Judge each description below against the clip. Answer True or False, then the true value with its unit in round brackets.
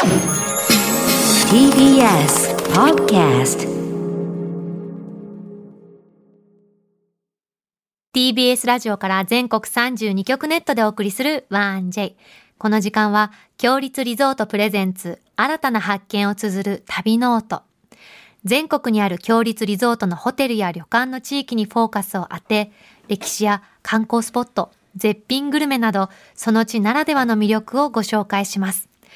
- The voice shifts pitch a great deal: False (3.1 semitones)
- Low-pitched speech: False (210 Hz)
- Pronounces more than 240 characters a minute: True (260 characters per minute)